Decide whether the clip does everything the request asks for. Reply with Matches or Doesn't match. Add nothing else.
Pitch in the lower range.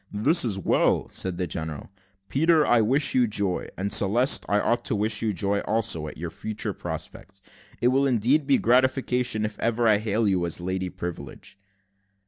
Matches